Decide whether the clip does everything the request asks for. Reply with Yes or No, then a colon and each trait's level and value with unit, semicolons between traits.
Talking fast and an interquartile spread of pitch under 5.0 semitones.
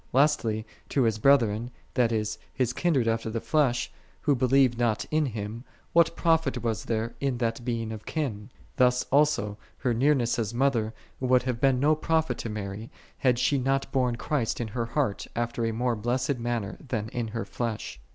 No: average, 190 wpm; average, 3.2 semitones